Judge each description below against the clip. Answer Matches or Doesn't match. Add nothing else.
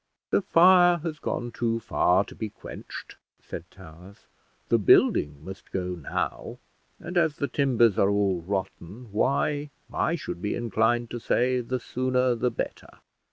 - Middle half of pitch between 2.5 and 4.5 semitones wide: Doesn't match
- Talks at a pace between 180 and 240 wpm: Doesn't match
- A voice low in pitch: Matches